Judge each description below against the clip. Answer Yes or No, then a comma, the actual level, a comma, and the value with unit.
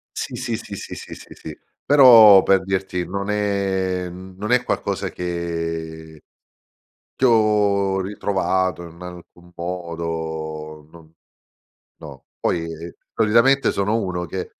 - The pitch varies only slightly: No, average, 3.4 semitones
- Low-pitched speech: Yes, very low, 95 Hz